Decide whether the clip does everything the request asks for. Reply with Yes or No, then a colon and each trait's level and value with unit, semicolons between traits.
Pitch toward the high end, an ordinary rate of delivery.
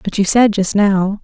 No: high, 200 Hz; fast, 245 wpm